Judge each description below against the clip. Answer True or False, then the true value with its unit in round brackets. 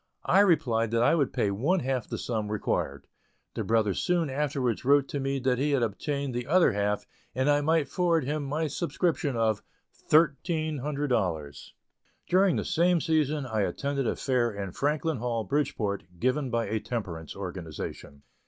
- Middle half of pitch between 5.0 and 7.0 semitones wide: True (5.4 semitones)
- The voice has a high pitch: False (130 Hz)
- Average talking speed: True (170 wpm)